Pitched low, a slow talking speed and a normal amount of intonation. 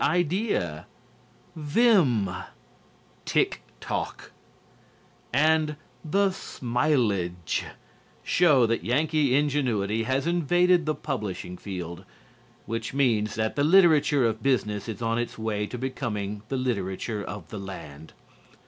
No: low, 125 Hz; slow, 110 wpm; wide, 6.4 semitones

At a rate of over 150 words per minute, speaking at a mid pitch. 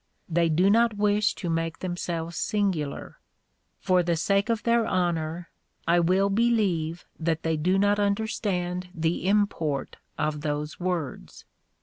No: slow, 135 wpm; medium, 180 Hz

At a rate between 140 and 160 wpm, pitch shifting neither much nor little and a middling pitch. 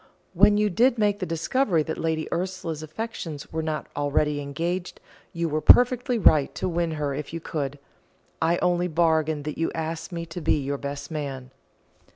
No: average, 180 wpm; average, 3.0 semitones; medium, 160 Hz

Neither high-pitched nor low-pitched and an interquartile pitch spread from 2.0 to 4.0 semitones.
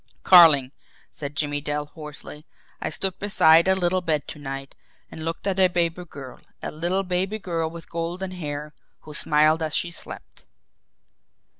Yes: medium, 165 Hz; average, 3.2 semitones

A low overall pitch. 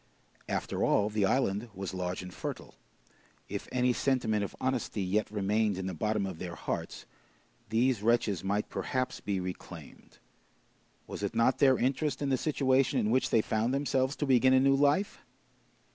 Yes: low, 115 Hz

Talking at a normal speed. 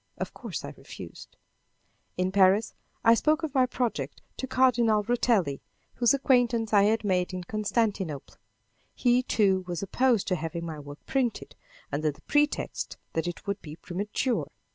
Yes: average, 155 wpm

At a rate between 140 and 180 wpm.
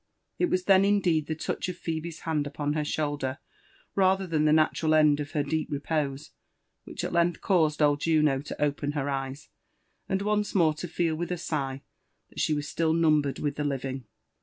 No: average, 195 wpm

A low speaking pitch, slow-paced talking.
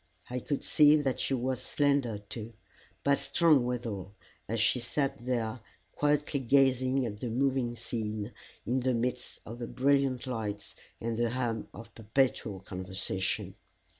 No: low, 120 Hz; average, 145 wpm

